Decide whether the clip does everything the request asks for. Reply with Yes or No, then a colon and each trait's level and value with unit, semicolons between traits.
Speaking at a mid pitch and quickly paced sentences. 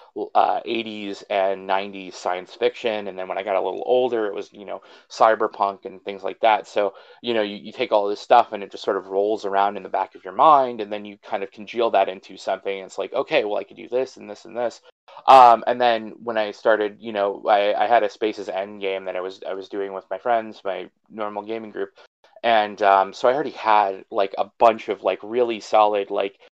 No: low, 105 Hz; fast, 245 wpm